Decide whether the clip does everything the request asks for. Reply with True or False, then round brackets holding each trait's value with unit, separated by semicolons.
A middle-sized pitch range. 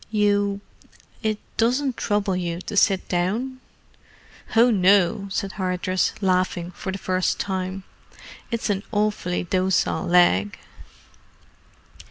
False (2.3 semitones)